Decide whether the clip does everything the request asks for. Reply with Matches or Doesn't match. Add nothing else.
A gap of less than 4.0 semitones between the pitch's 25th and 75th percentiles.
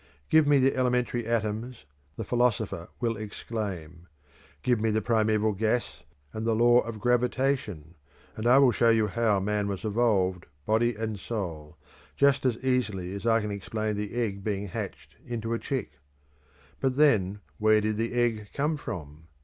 Matches